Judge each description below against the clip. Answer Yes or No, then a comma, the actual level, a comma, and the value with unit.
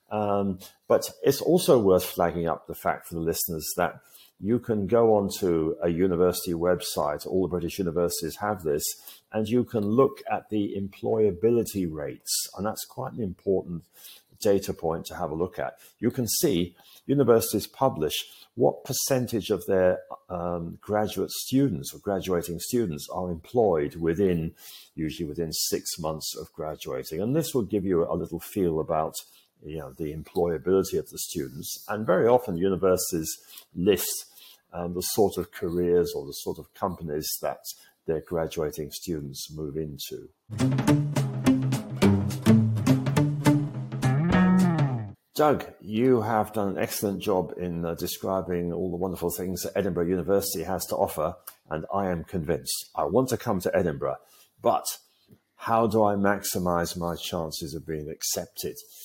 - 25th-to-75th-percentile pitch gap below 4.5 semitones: No, average, 4.8 semitones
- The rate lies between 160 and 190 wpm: No, average, 150 wpm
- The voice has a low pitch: Yes, very low, 95 Hz